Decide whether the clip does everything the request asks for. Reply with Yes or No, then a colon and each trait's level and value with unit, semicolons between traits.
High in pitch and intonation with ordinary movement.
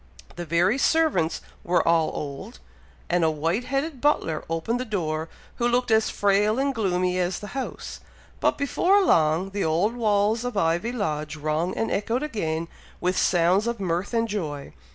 No: high, 195 Hz; wide, 6.2 semitones